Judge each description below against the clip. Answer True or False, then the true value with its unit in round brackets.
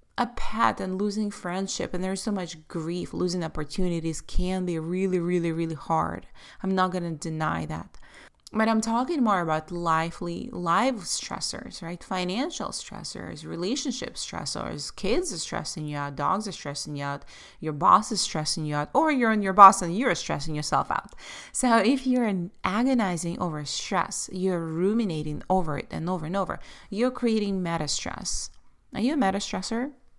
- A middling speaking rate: True (170 wpm)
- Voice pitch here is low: False (185 Hz)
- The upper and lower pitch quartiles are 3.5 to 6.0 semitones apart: True (4.6 semitones)